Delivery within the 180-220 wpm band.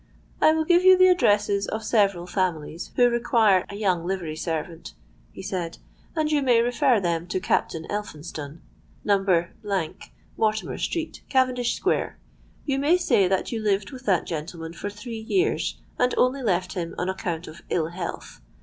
No: average, 165 wpm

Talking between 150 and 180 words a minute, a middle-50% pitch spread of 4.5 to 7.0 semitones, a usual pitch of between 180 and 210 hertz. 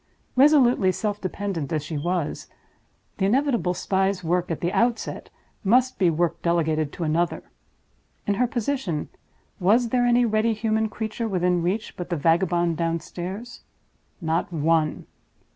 No: average, 140 wpm; average, 5.1 semitones; medium, 185 Hz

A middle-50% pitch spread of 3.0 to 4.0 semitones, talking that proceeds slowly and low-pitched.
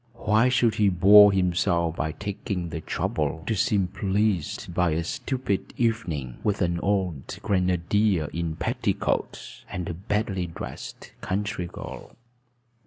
Yes: average, 3.5 semitones; slow, 130 wpm; very low, 95 Hz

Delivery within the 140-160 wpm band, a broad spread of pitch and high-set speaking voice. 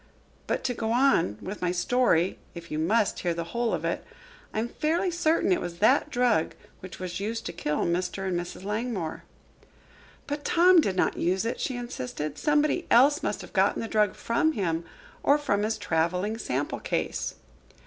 No: average, 185 wpm; wide, 6.2 semitones; high, 210 Hz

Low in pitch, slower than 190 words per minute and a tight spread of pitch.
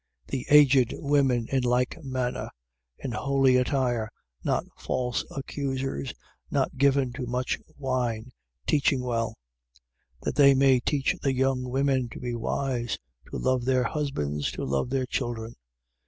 Yes: low, 130 Hz; average, 145 wpm; narrow, 2.0 semitones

